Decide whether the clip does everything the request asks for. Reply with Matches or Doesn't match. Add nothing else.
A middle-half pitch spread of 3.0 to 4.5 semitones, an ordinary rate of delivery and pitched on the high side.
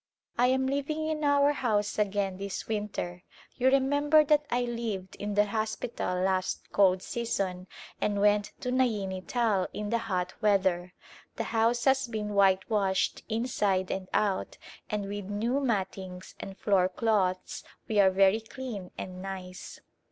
Matches